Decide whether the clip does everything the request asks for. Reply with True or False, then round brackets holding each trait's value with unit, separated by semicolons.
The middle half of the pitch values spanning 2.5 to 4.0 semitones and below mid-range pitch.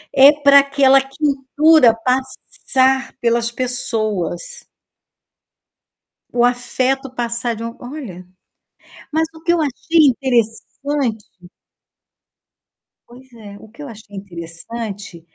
False (3.6 semitones; 250 Hz)